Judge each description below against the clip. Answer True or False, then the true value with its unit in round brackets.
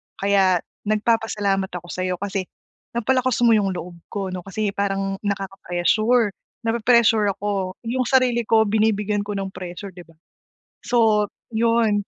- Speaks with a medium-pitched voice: False (205 Hz)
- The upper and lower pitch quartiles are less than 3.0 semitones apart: True (2.6 semitones)